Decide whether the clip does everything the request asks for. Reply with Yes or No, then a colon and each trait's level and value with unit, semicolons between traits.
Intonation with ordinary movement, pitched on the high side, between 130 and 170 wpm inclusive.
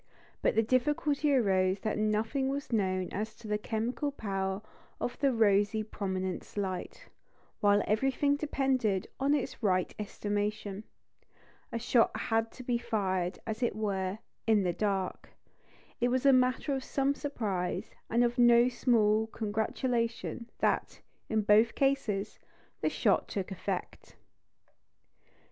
Yes: average, 3.7 semitones; high, 220 Hz; slow, 135 wpm